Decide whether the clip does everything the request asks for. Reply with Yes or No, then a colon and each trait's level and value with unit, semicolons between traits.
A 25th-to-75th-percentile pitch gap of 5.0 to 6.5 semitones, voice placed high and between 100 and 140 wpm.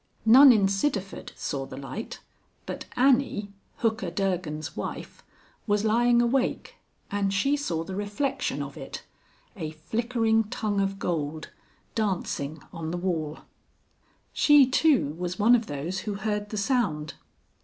Yes: wide, 5.5 semitones; high, 200 Hz; slow, 135 wpm